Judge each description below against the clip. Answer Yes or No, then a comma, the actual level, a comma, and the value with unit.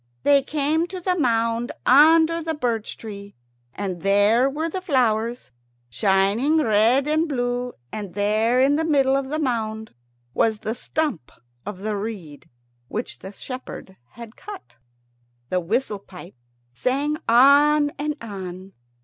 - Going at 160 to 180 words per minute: No, average, 140 wpm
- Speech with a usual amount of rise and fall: No, wide, 5.9 semitones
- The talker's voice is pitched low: No, high, 240 Hz